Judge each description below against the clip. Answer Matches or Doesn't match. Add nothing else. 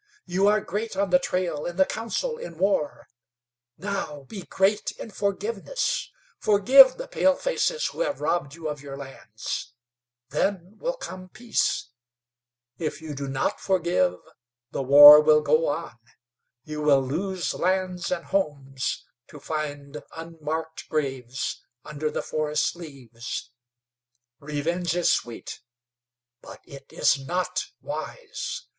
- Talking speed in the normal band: Doesn't match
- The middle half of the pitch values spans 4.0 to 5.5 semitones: Matches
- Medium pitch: Matches